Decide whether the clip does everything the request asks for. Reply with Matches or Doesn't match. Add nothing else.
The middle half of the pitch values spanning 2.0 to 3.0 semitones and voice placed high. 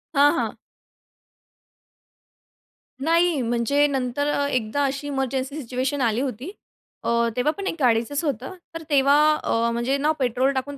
Matches